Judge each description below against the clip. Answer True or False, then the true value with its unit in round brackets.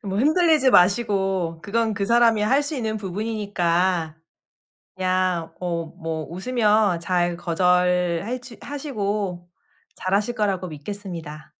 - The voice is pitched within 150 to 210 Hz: True (195 Hz)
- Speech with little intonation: False (4.0 semitones)